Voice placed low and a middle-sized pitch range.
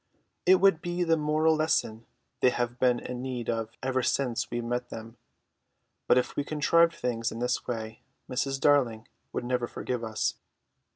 Yes: low, 125 Hz; average, 4.0 semitones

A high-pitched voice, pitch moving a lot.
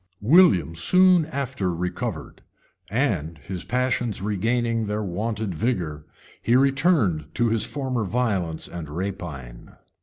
No: low, 105 Hz; wide, 6.3 semitones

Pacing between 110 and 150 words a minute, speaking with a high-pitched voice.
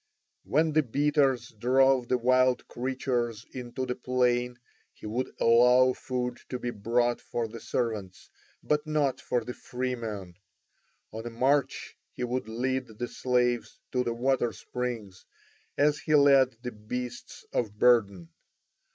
No: average, 140 wpm; low, 125 Hz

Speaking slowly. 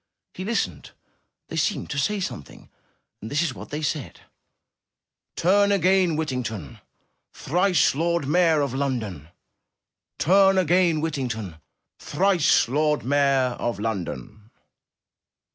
Yes: slow, 115 wpm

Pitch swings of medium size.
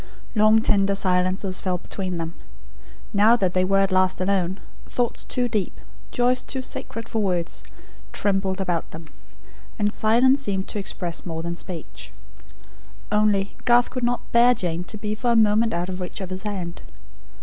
Yes: average, 3.3 semitones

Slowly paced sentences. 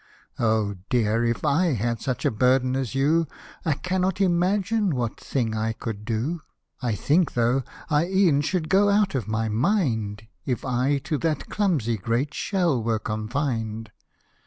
No: average, 160 wpm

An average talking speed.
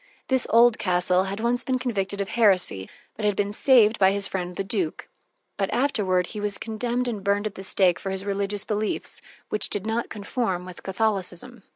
Yes: average, 190 wpm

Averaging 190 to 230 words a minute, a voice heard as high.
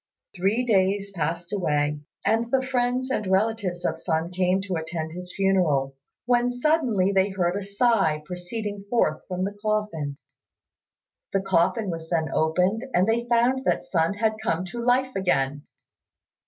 No: average, 155 wpm; high, 195 Hz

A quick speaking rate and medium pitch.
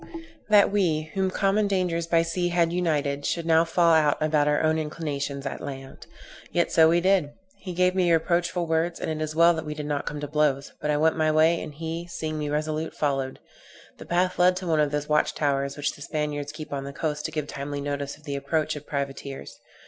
Yes: fast, 225 wpm; medium, 155 Hz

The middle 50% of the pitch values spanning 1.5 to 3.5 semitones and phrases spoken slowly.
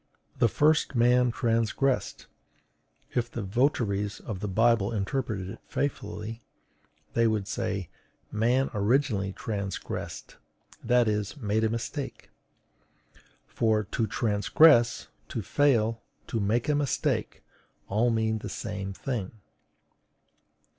Yes: average, 3.0 semitones; slow, 110 wpm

